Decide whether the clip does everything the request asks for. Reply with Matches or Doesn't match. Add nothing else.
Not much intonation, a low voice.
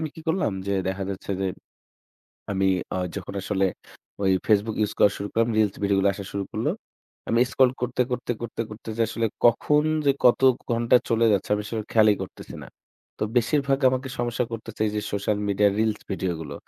Doesn't match